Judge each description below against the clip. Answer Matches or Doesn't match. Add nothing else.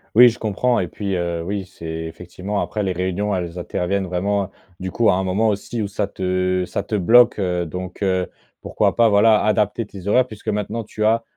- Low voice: Matches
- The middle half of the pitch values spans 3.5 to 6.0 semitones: Doesn't match